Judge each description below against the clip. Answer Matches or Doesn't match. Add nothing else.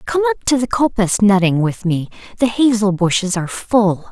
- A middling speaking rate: Matches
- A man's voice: Doesn't match